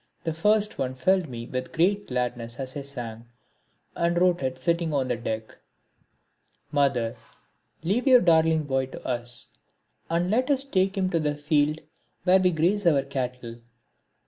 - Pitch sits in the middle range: Yes, medium, 150 Hz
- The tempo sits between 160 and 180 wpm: Yes, average, 165 wpm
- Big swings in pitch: Yes, wide, 6.1 semitones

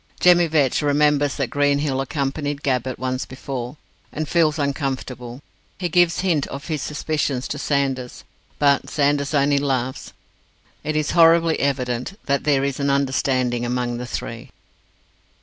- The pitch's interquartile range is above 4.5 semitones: No, narrow, 2.4 semitones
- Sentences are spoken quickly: No, average, 140 wpm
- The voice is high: No, medium, 140 Hz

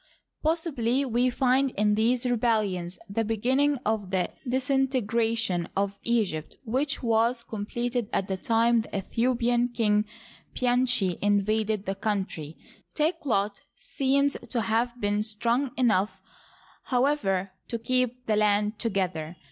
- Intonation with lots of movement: No, average, 3.5 semitones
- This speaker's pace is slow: Yes, slow, 125 wpm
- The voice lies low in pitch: No, high, 225 Hz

